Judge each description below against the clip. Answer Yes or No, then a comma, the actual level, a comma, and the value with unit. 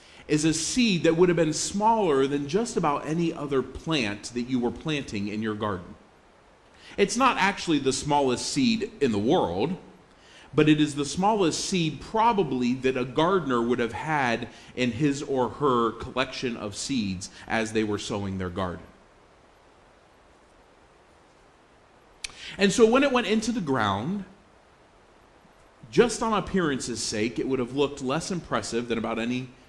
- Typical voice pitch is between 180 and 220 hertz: No, low, 135 Hz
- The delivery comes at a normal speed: Yes, average, 155 wpm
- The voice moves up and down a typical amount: No, wide, 7.6 semitones